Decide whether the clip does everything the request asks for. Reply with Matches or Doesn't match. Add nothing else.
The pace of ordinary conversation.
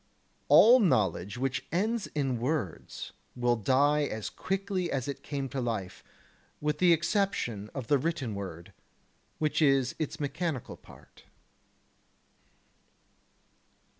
Doesn't match